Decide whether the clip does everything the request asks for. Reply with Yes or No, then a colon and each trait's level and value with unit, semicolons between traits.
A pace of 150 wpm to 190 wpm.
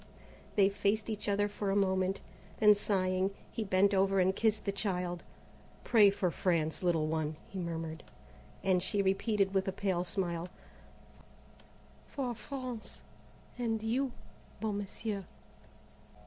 No: slow, 135 wpm